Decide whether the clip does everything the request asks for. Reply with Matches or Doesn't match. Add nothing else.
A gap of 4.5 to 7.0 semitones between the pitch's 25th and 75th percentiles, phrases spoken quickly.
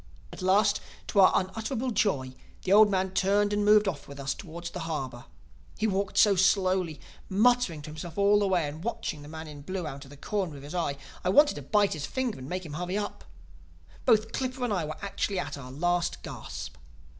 Matches